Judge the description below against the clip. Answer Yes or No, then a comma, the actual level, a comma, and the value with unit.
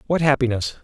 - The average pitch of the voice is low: Yes, low, 130 Hz